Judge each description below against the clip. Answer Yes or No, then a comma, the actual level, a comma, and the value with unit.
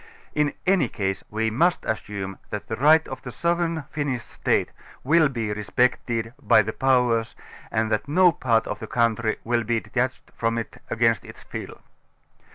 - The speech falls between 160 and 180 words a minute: Yes, average, 165 wpm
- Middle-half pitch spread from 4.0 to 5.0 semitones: Yes, average, 4.3 semitones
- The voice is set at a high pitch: No, low, 120 Hz